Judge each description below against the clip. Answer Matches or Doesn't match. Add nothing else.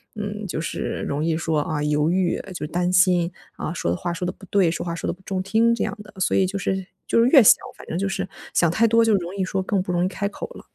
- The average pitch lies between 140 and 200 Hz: Matches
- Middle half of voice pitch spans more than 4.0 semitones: Doesn't match